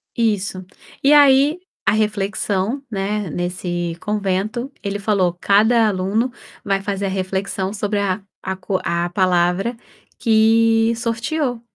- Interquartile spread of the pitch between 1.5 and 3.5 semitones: Yes, average, 3.1 semitones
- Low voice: No, high, 205 Hz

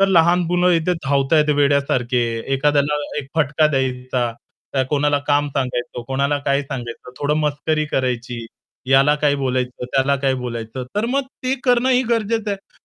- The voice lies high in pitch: No, medium, 140 Hz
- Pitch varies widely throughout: No, average, 3.5 semitones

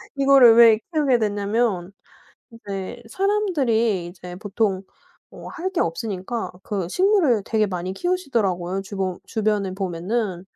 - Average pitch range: Yes, average, 4.3 semitones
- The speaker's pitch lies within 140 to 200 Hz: No, high, 215 Hz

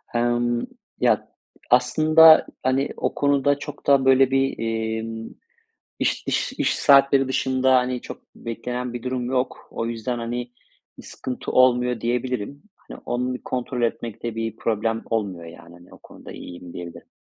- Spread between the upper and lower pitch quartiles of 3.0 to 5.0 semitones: No, narrow, 2.6 semitones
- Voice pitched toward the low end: Yes, low, 125 Hz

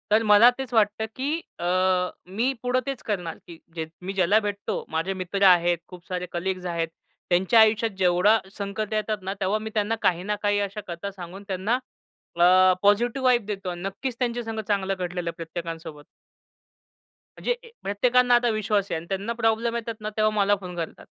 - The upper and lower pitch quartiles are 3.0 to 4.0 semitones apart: Yes, average, 3.5 semitones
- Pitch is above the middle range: Yes, high, 200 Hz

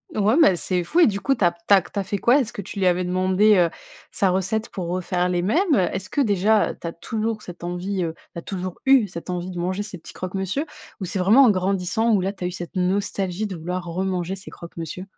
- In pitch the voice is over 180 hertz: Yes, high, 190 Hz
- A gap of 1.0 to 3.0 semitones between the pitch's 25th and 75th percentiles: Yes, narrow, 2.5 semitones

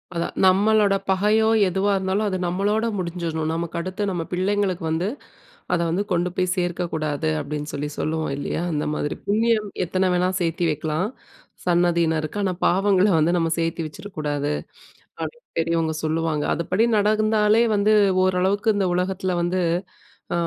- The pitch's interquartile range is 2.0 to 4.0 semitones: Yes, average, 3.5 semitones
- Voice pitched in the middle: Yes, medium, 180 Hz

